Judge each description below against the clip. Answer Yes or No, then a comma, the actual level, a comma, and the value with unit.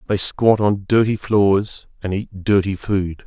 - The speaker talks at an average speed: Yes, average, 165 wpm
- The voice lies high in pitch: No, low, 100 Hz